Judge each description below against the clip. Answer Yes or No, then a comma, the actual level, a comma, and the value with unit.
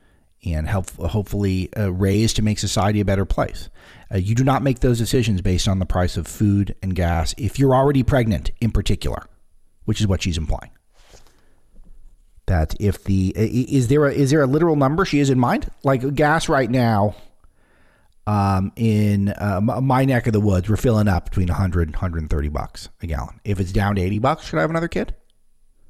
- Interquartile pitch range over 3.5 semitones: Yes, average, 5.1 semitones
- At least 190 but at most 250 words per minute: Yes, average, 195 wpm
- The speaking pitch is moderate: No, low, 100 Hz